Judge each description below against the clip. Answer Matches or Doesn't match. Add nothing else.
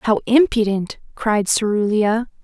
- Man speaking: Doesn't match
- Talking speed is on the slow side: Matches